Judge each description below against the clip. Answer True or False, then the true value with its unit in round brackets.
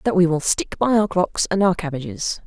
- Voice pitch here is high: False (175 Hz)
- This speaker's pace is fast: True (245 wpm)